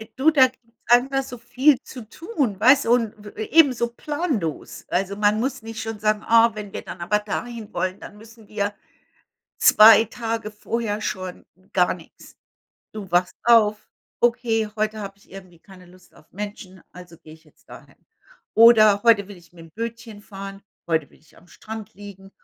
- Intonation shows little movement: No, average, 3.2 semitones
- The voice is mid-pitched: No, high, 215 Hz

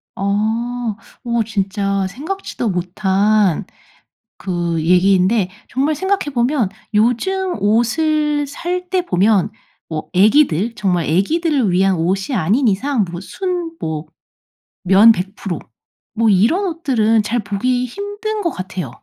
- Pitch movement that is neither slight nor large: No, wide, 7.7 semitones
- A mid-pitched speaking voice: No, high, 220 Hz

